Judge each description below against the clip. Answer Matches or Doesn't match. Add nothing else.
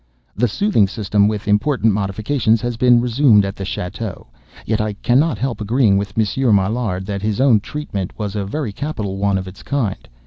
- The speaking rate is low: Doesn't match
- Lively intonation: Doesn't match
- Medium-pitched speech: Doesn't match